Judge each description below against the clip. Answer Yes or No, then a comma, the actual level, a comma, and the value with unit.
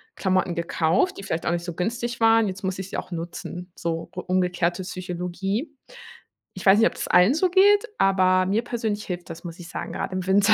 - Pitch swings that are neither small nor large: Yes, average, 3.4 semitones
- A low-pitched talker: No, medium, 185 Hz